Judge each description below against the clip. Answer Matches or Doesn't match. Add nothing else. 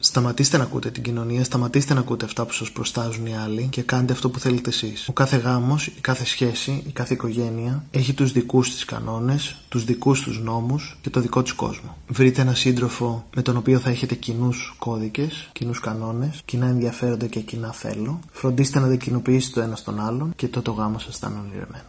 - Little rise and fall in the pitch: Matches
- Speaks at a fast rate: Matches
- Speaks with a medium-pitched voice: Doesn't match